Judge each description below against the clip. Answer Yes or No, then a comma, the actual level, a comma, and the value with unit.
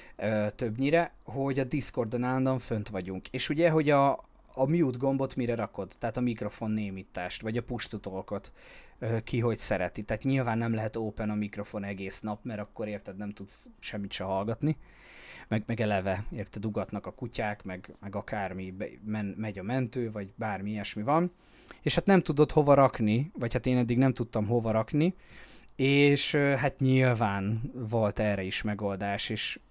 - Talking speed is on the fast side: Yes, fast, 175 wpm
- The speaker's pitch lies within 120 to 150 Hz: No, low, 110 Hz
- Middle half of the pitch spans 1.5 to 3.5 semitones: No, average, 4.2 semitones